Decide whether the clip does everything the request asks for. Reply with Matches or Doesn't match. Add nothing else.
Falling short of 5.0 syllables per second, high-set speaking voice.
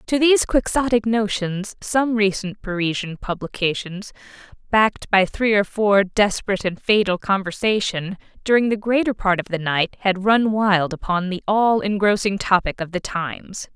Matches